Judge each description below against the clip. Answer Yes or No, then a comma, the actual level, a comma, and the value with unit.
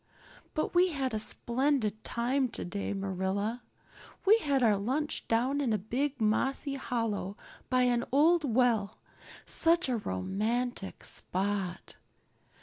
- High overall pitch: Yes, high, 240 Hz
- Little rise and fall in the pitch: No, average, 5.0 semitones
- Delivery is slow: Yes, slow, 125 wpm